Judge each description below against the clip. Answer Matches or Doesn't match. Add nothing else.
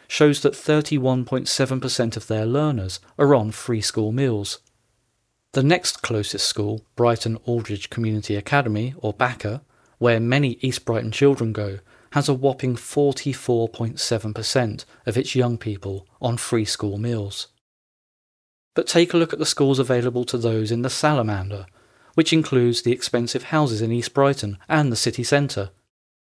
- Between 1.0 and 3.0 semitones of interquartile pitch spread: Doesn't match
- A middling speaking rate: Matches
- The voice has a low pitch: Matches